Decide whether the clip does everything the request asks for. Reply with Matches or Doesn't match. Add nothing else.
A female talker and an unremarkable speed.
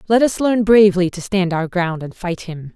Doesn't match